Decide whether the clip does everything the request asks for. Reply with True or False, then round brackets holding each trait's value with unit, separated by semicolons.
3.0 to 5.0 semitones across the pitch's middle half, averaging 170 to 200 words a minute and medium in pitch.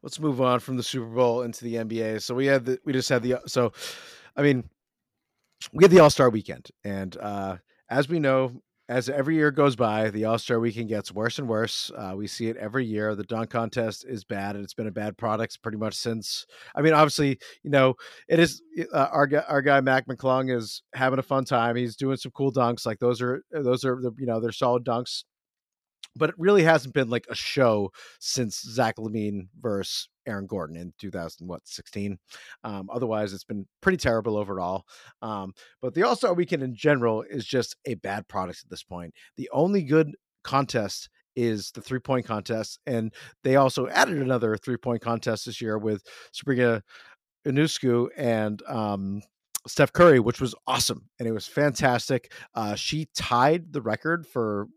False (3.8 semitones; 195 wpm; 120 Hz)